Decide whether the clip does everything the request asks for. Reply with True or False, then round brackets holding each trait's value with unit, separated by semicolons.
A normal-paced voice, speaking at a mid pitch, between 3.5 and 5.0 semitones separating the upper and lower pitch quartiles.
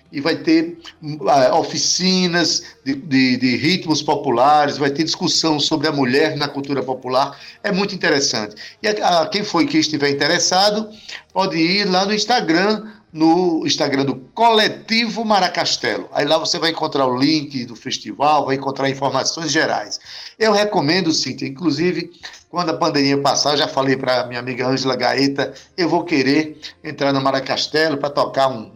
True (165 wpm; 155 Hz; 4.3 semitones)